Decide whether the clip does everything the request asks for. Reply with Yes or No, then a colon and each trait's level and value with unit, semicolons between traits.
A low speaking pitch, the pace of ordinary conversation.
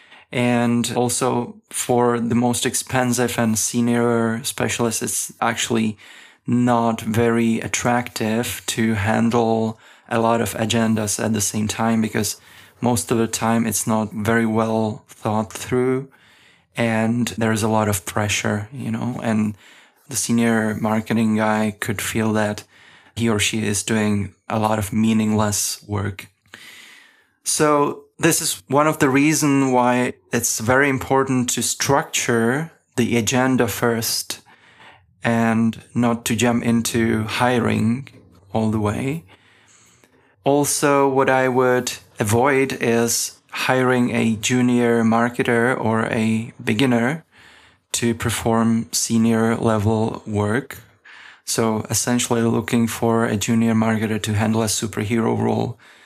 Yes: low, 115 Hz; average, 125 wpm